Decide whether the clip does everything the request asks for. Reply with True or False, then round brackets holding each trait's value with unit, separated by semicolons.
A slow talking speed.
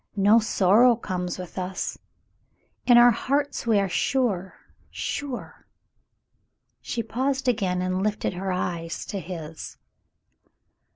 True (130 wpm)